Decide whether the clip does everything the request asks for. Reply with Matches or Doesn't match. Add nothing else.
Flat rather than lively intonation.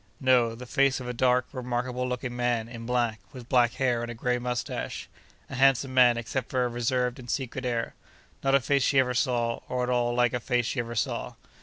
Matches